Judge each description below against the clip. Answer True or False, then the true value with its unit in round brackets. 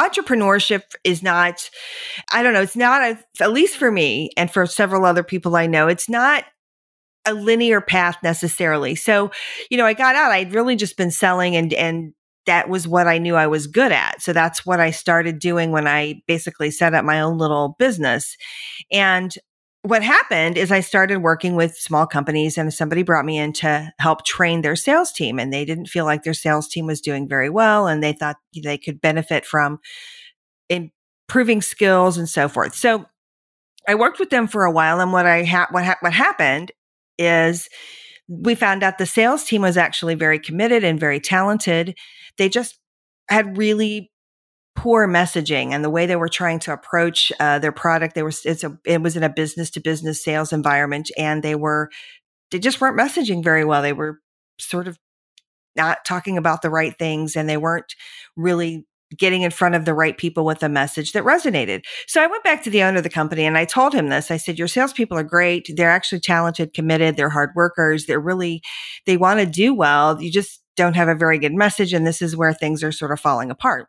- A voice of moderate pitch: True (170 Hz)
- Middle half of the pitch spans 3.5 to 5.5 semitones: True (4.0 semitones)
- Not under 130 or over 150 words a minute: False (205 wpm)